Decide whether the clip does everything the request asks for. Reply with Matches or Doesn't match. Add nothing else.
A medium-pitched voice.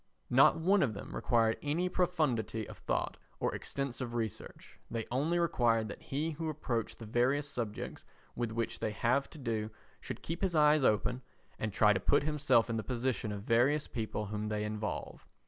Doesn't match